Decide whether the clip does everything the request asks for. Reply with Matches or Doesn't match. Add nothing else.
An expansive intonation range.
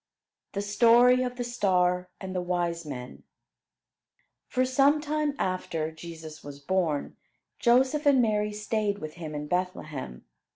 Matches